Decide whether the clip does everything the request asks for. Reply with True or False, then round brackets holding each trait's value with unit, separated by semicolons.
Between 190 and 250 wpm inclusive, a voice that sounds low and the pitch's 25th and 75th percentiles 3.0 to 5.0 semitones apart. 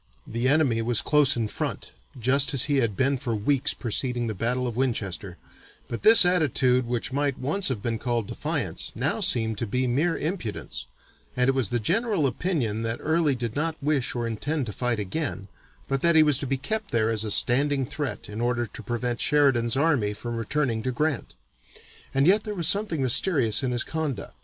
True (200 wpm; 130 Hz; 4.2 semitones)